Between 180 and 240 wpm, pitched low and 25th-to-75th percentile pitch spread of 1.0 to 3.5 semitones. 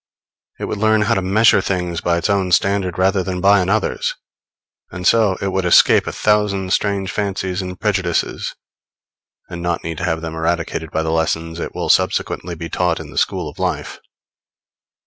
Yes: average, 185 wpm; very low, 95 Hz; narrow, 2.6 semitones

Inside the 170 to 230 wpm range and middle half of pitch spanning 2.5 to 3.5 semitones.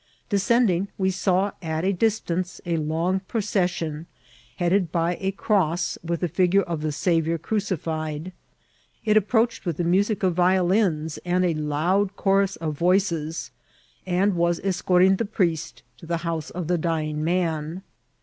No: average, 160 wpm; average, 2.8 semitones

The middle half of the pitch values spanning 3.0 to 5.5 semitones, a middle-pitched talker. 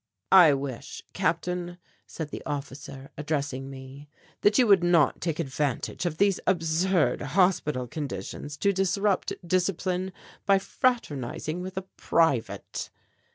Yes: average, 5.0 semitones; medium, 165 Hz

